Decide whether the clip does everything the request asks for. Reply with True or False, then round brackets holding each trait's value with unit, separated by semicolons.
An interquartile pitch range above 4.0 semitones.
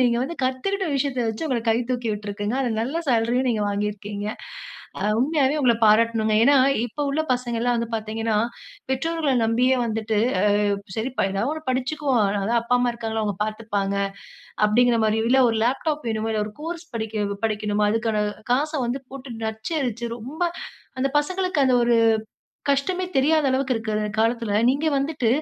False (3.7 semitones)